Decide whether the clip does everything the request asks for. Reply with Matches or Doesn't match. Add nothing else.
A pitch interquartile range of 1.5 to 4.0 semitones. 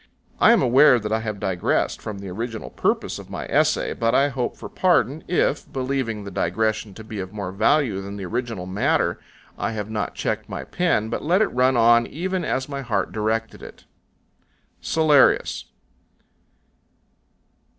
Doesn't match